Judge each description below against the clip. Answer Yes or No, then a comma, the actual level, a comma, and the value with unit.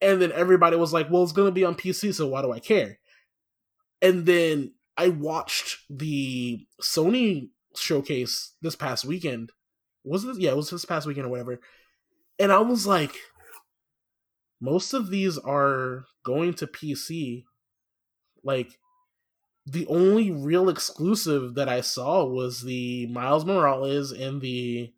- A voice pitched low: No, medium, 155 Hz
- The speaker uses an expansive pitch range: Yes, wide, 6.1 semitones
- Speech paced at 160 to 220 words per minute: No, average, 150 wpm